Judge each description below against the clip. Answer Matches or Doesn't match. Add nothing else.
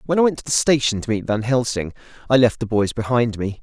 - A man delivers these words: Matches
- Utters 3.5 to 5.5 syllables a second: Doesn't match